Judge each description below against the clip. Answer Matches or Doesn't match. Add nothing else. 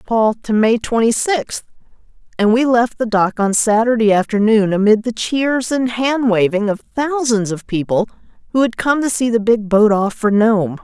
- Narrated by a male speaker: Doesn't match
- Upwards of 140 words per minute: Matches